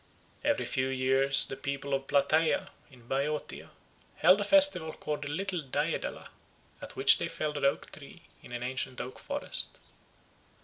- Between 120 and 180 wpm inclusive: Yes, average, 160 wpm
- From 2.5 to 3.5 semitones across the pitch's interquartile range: Yes, average, 2.9 semitones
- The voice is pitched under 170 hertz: Yes, medium, 140 Hz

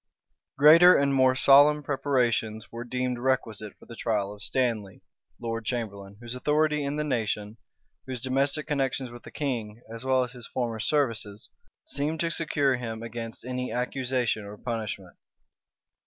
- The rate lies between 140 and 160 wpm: Yes, average, 155 wpm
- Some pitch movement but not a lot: Yes, average, 3.6 semitones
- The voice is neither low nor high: No, low, 125 Hz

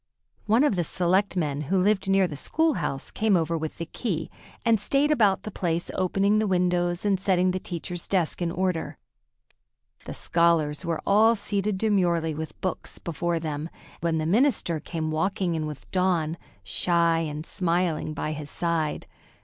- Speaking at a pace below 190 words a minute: Yes, average, 165 wpm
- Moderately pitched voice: Yes, medium, 175 Hz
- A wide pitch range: No, average, 3.2 semitones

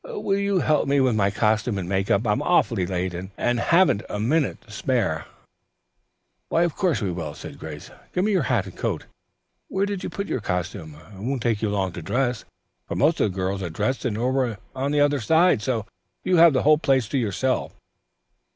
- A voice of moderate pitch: No, low, 120 Hz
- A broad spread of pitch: Yes, wide, 7.2 semitones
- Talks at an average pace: No, fast, 215 wpm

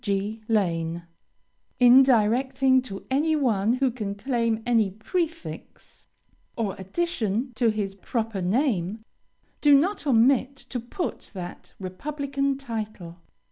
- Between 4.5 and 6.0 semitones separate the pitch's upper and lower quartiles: Yes, average, 5.1 semitones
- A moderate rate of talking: No, slow, 115 wpm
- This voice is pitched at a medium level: No, high, 230 Hz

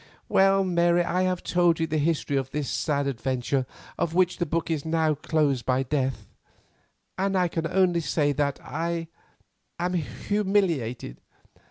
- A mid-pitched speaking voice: Yes, medium, 165 Hz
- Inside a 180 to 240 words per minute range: No, average, 155 wpm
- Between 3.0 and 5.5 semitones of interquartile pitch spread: Yes, average, 3.8 semitones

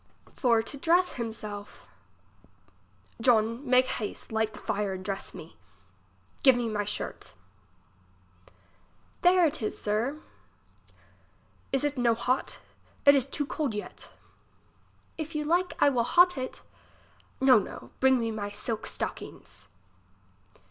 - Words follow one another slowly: Yes, slow, 130 wpm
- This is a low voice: No, high, 245 Hz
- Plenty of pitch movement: No, average, 4.9 semitones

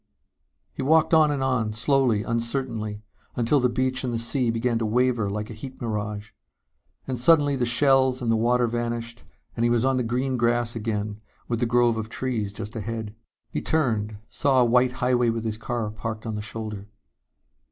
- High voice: No, low, 120 Hz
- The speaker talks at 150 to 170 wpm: No, average, 190 wpm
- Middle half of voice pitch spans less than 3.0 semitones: Yes, narrow, 2.5 semitones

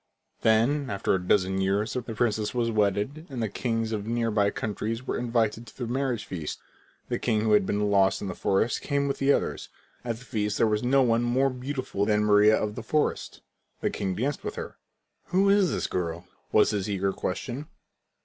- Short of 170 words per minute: No, fast, 205 wpm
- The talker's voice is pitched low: Yes, low, 110 Hz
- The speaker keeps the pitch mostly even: No, average, 3.4 semitones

